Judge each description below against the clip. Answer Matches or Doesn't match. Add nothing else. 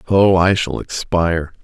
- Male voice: Matches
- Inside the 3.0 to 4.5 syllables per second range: Matches